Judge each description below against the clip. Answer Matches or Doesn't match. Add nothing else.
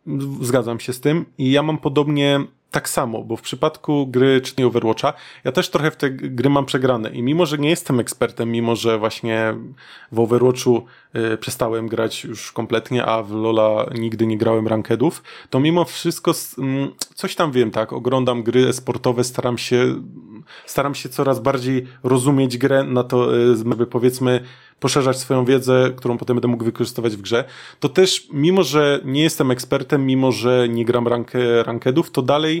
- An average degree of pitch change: Matches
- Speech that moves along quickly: Matches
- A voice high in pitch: Doesn't match